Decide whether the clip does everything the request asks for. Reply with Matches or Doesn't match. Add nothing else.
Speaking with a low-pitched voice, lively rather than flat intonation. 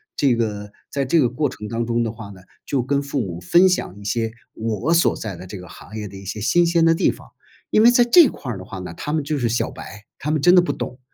Matches